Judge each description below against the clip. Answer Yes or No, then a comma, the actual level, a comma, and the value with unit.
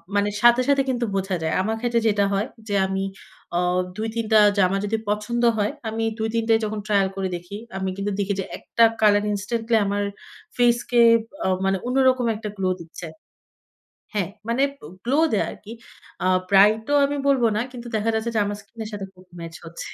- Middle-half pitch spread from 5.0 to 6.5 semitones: No, average, 3.0 semitones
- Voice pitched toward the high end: Yes, high, 210 Hz